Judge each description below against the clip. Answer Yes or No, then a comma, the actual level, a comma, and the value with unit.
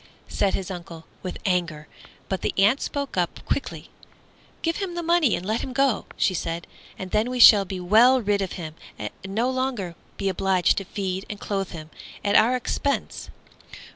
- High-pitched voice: Yes, high, 200 Hz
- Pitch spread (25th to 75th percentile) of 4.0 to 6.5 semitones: Yes, wide, 5.5 semitones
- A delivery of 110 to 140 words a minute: No, average, 185 wpm